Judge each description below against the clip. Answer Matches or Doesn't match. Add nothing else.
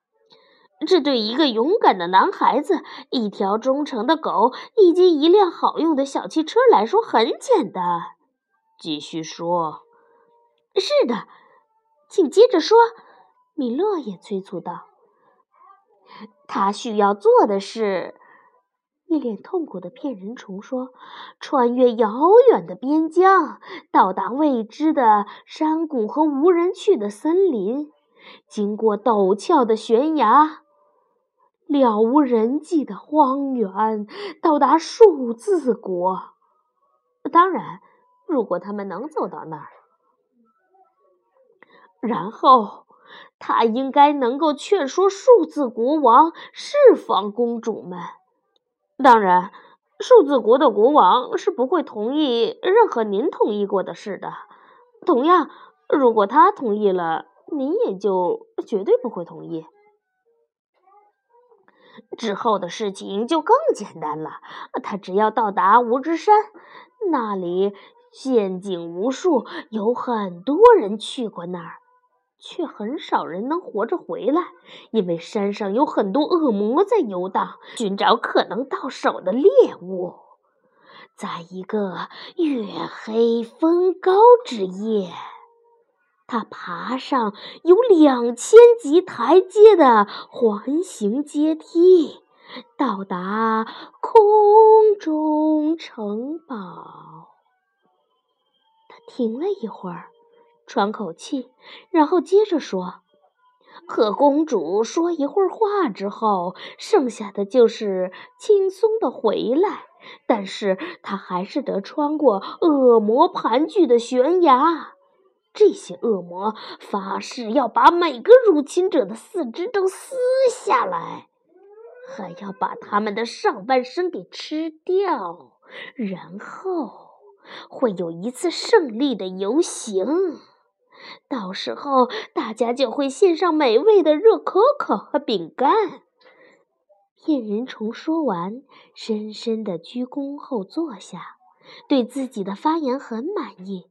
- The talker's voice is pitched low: Doesn't match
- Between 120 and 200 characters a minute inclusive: Matches